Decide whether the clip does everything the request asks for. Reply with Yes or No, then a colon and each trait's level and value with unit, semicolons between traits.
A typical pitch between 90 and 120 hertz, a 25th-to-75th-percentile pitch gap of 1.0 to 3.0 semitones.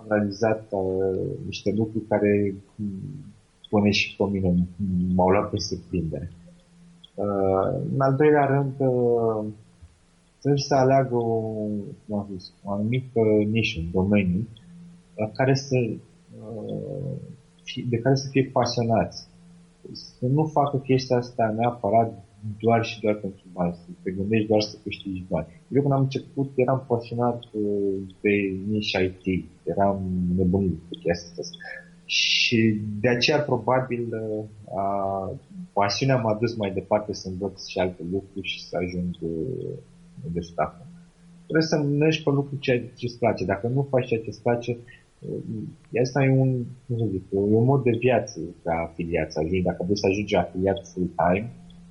No: low, 105 Hz; average, 5.1 semitones